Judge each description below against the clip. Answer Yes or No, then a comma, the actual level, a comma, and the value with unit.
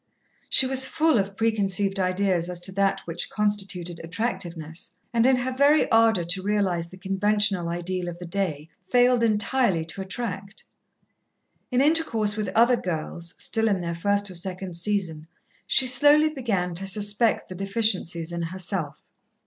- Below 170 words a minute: Yes, average, 155 wpm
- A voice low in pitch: No, high, 195 Hz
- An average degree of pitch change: Yes, average, 4.3 semitones